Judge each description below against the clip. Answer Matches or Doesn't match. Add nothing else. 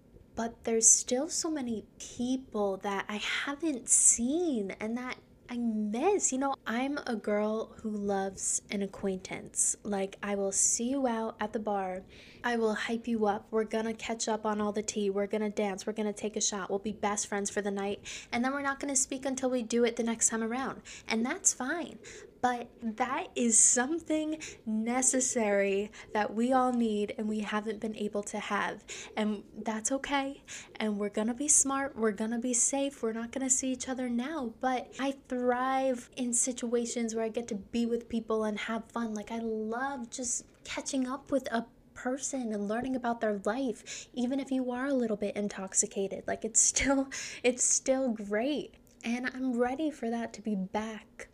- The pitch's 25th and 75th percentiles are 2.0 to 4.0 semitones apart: Matches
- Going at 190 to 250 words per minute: Matches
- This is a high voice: Matches